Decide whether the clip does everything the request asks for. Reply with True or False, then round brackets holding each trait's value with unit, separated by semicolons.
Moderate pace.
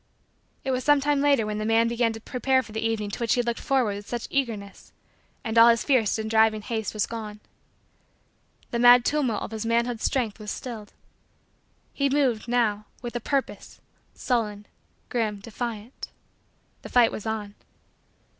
True (175 wpm)